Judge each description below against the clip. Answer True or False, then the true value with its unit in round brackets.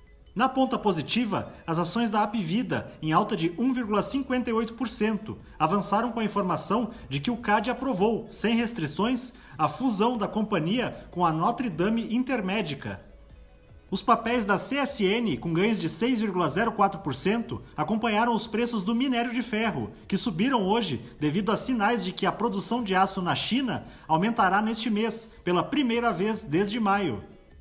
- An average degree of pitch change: True (3.8 semitones)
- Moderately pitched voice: False (215 Hz)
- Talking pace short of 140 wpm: False (150 wpm)